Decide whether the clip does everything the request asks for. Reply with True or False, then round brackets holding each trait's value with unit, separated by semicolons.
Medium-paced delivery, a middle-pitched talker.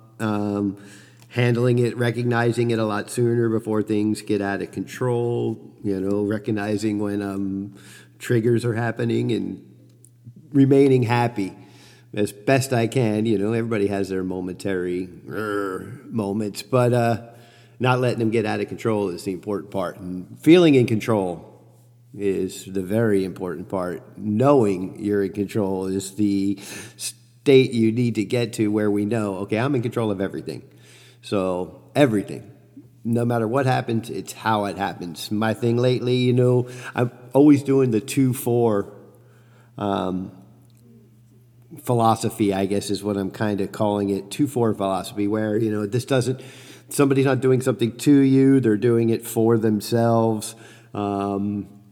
False (155 wpm; 110 Hz)